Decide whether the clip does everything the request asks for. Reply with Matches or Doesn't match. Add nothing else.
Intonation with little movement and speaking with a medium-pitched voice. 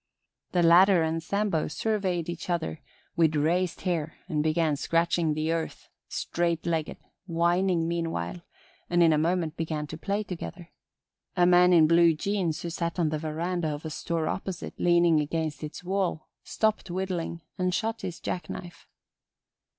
Matches